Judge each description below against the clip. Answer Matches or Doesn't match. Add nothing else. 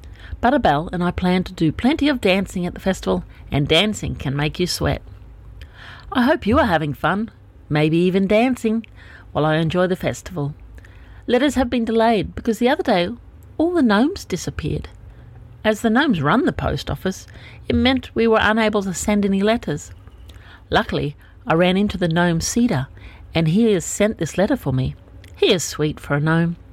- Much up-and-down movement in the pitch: Matches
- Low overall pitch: Doesn't match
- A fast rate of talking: Doesn't match